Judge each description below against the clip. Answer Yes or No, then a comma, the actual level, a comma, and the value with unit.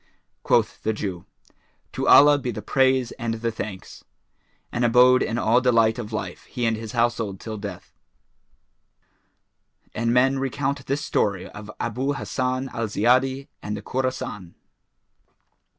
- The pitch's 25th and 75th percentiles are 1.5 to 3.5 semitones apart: Yes, average, 3.1 semitones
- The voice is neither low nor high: No, low, 120 Hz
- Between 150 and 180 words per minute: No, average, 140 wpm